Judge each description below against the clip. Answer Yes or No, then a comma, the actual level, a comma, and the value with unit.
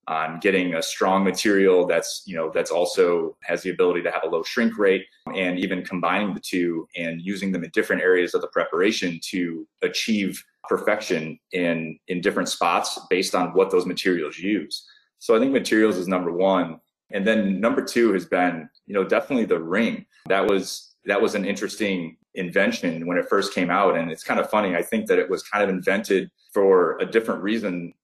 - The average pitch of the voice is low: Yes, low, 110 Hz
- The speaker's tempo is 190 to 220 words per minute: Yes, average, 200 wpm